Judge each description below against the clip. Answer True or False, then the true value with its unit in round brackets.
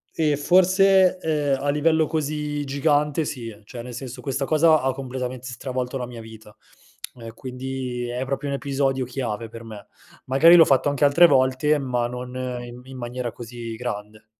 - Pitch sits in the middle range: False (130 Hz)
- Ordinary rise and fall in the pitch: True (3.2 semitones)